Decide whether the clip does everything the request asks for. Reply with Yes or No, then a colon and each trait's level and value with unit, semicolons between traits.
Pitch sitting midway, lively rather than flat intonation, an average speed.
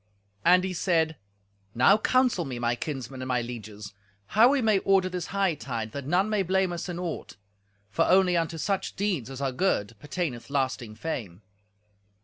Yes: medium, 165 Hz; wide, 7.3 semitones; average, 170 wpm